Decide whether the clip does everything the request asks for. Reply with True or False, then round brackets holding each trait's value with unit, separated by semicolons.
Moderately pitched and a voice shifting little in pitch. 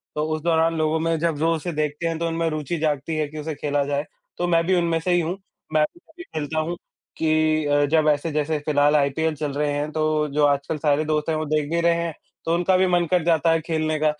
True (155 Hz; 1.8 semitones)